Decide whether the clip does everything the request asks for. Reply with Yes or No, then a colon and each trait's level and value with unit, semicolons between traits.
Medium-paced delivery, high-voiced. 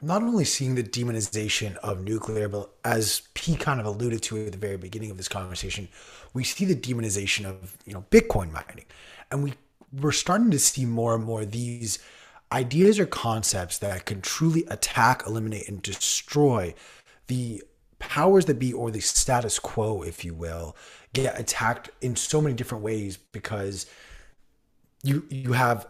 No: average, 165 wpm; low, 115 Hz